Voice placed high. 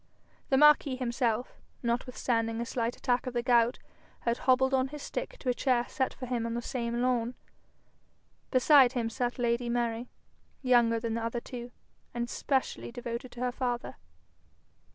Yes: high, 245 Hz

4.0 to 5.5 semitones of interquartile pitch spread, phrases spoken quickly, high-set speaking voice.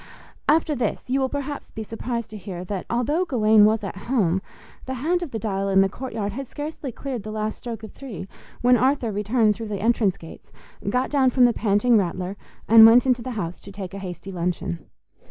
Yes: average, 4.3 semitones; fast, 210 wpm; high, 225 Hz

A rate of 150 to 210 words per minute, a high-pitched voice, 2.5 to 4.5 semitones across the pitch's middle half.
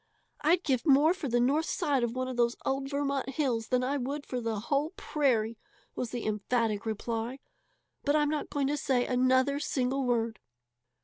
Yes: average, 185 wpm; very high, 260 Hz; average, 3.2 semitones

